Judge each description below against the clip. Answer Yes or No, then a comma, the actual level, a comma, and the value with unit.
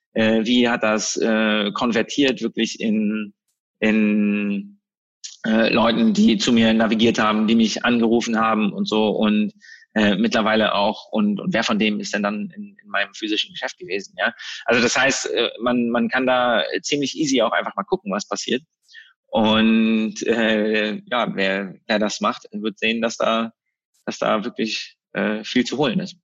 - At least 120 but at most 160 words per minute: No, average, 170 wpm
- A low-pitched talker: Yes, low, 115 Hz